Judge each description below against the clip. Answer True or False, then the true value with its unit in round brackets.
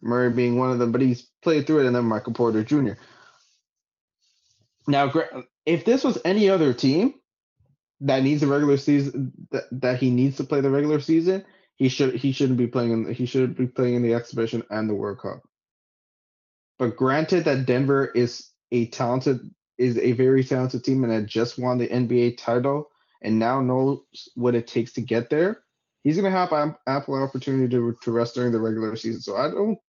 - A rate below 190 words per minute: False (195 wpm)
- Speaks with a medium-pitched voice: False (130 Hz)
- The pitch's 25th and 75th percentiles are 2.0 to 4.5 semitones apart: True (2.9 semitones)